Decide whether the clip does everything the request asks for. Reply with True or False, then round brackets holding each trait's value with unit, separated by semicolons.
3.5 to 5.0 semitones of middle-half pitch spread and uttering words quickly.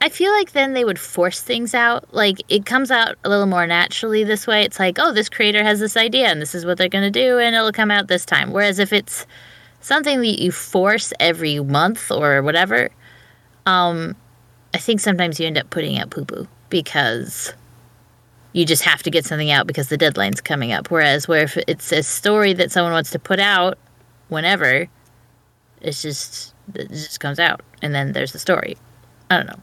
False (5.6 semitones; 210 wpm)